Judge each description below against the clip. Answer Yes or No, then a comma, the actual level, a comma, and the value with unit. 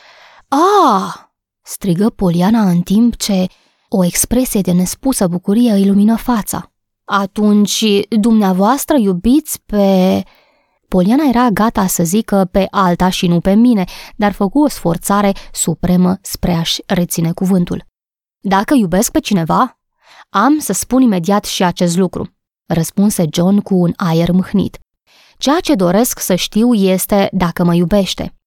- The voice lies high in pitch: Yes, high, 200 Hz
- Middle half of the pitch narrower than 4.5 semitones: Yes, average, 3.6 semitones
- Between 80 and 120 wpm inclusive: No, average, 135 wpm